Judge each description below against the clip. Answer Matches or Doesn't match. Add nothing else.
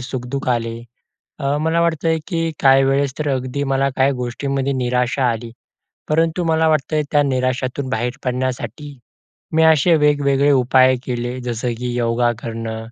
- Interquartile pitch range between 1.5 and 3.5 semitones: Matches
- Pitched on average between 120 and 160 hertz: Matches